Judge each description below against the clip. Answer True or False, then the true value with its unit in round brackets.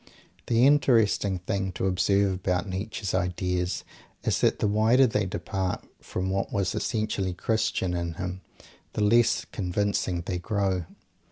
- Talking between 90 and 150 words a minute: True (140 wpm)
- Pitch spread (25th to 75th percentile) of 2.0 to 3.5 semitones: True (2.6 semitones)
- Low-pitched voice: True (95 Hz)